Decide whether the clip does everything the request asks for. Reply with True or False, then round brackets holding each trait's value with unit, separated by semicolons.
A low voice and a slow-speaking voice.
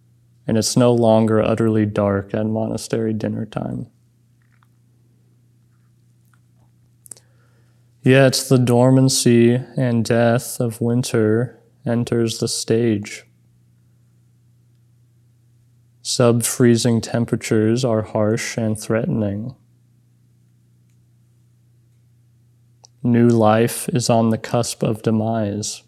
True (120 Hz; 80 wpm)